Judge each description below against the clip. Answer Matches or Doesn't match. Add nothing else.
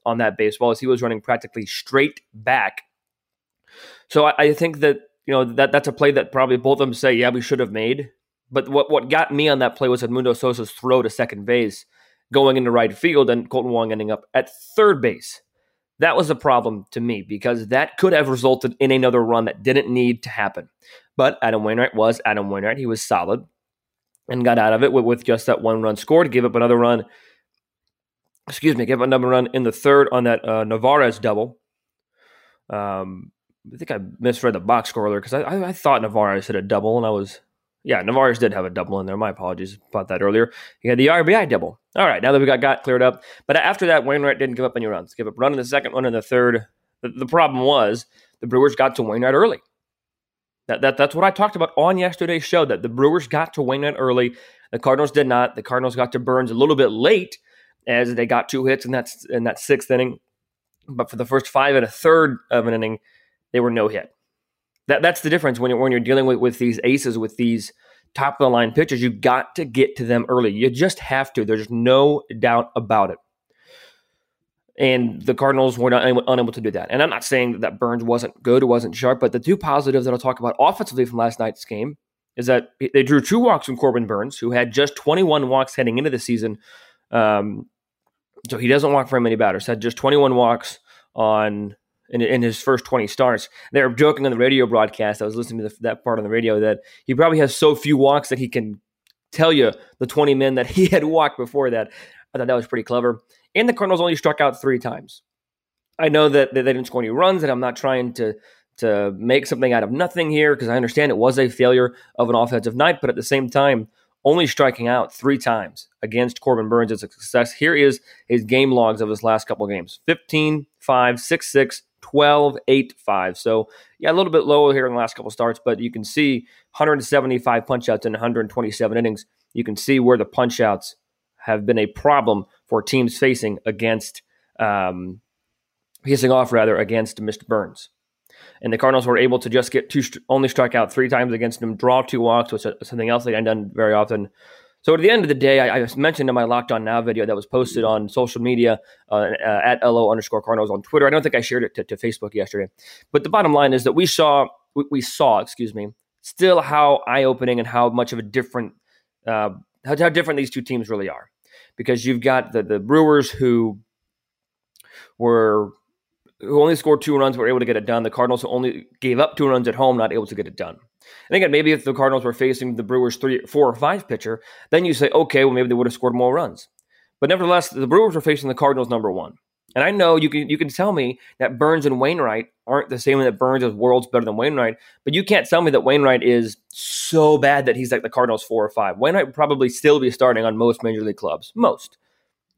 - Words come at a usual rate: Doesn't match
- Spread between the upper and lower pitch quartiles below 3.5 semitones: Matches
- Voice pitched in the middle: Doesn't match